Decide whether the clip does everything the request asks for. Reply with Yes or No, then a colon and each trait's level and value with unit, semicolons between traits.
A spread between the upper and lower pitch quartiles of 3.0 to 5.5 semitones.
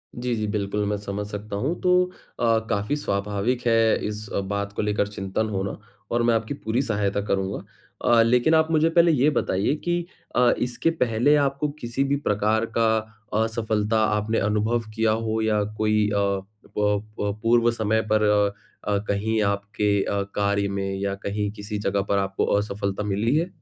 No: narrow, 2.6 semitones